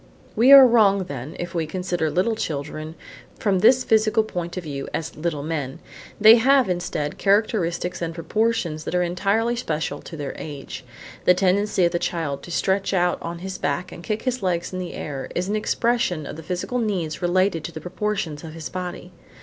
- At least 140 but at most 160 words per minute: No, average, 190 wpm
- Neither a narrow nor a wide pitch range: Yes, average, 4.7 semitones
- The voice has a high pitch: No, medium, 180 Hz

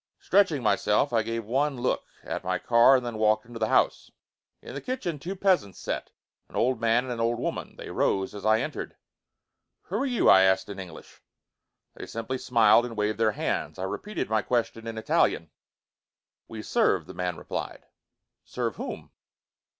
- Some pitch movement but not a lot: Yes, average, 3.5 semitones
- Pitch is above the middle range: No, low, 115 Hz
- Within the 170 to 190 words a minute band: Yes, average, 180 wpm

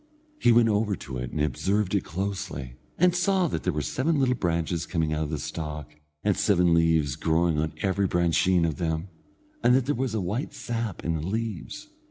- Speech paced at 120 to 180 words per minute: No, fast, 205 wpm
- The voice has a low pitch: Yes, very low, 90 Hz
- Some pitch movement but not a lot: No, wide, 5.8 semitones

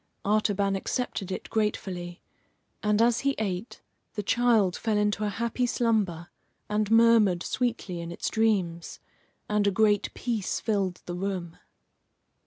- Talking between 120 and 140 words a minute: Yes, slow, 135 wpm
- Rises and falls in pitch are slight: No, average, 3.2 semitones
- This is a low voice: No, high, 210 Hz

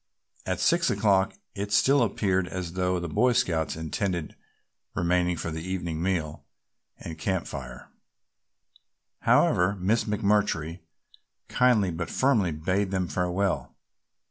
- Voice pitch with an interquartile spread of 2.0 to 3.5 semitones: Yes, average, 3.1 semitones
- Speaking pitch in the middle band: No, very low, 90 Hz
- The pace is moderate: No, slow, 120 wpm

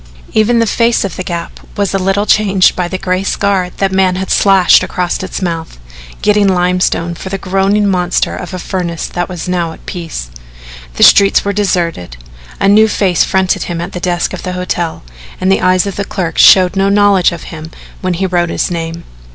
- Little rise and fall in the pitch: Yes, narrow, 2.0 semitones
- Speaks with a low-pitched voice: No, medium, 185 Hz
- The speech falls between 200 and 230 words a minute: Yes, fast, 205 wpm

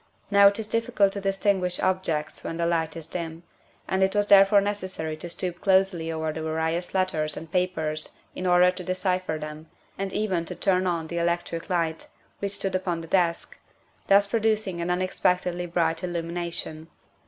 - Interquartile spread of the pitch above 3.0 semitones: No, narrow, 2.6 semitones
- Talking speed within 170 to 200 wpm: Yes, average, 175 wpm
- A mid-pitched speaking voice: Yes, medium, 180 Hz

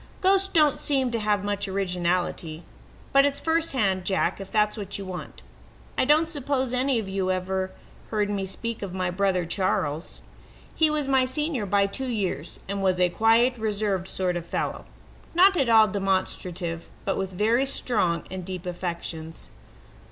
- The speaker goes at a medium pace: Yes, average, 170 wpm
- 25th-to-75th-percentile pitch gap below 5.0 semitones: No, wide, 5.6 semitones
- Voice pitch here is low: No, high, 200 Hz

